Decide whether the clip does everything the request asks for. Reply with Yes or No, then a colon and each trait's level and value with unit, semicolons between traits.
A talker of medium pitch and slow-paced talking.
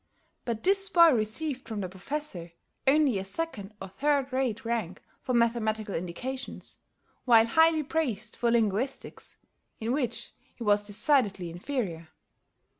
No: high, 235 Hz; slow, 130 wpm